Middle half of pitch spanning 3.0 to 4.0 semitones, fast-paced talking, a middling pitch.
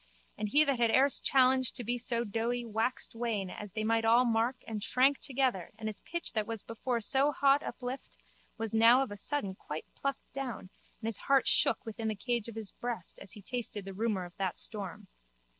No: average, 3.3 semitones; fast, 210 wpm; high, 230 Hz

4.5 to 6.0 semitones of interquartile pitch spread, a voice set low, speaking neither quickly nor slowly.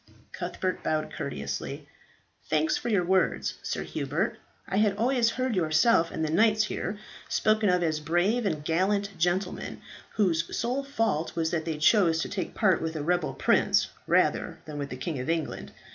No: average, 4.9 semitones; medium, 175 Hz; average, 175 wpm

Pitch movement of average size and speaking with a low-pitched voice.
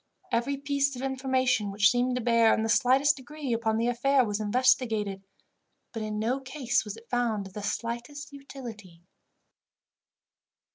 No: average, 3.4 semitones; high, 245 Hz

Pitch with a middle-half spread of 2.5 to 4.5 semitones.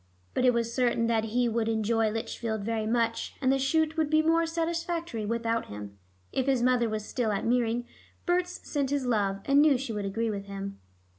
Yes: average, 3.9 semitones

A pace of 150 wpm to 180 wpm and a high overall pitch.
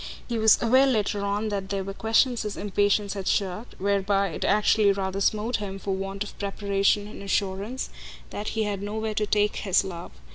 No: average, 190 wpm; high, 205 Hz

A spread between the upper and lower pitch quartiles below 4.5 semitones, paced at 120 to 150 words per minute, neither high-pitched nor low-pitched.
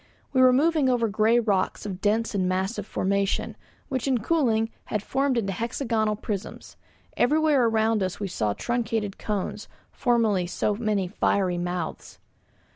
No: average, 3.6 semitones; average, 145 wpm; high, 220 Hz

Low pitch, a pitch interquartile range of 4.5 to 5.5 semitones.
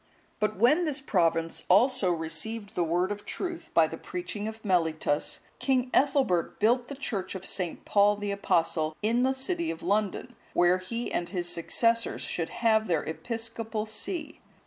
No: high, 205 Hz; average, 5.1 semitones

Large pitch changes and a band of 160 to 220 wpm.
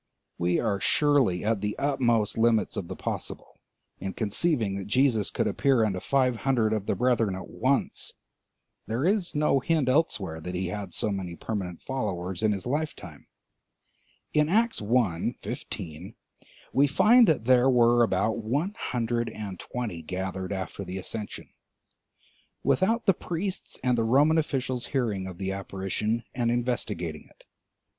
No: wide, 5.7 semitones; average, 150 wpm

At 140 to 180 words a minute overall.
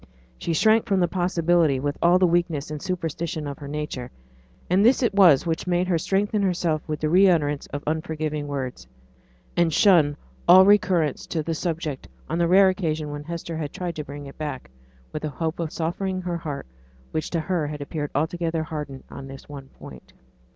No: average, 195 wpm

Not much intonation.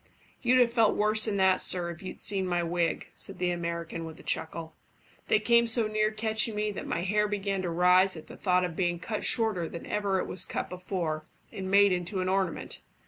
No: average, 3.4 semitones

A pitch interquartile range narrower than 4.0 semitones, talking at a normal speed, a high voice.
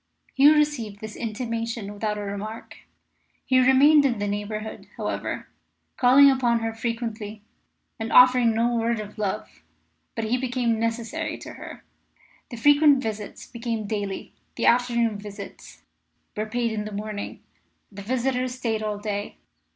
Yes: average, 2.9 semitones; average, 145 wpm; high, 230 Hz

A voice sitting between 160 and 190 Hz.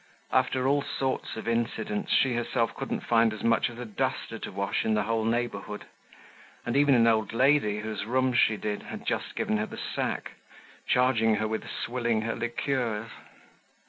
No: low, 115 Hz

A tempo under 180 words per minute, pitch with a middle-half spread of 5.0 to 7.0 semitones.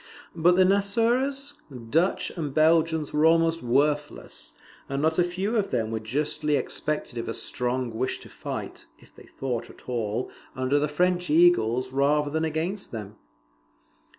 Yes: average, 155 wpm; wide, 5.4 semitones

